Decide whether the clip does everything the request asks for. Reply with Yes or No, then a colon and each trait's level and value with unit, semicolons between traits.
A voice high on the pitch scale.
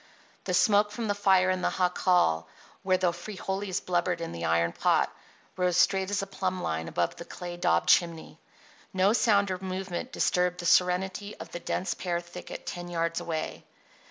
No: medium, 180 Hz